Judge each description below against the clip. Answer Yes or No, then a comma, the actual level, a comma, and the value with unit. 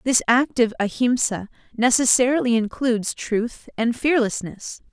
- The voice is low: No, high, 240 Hz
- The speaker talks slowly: Yes, slow, 100 wpm